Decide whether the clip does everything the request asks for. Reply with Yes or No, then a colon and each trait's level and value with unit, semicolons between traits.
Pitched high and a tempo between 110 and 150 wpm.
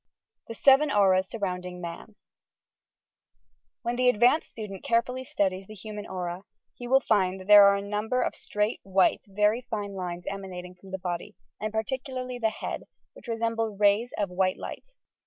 No: high, 210 Hz; average, 170 wpm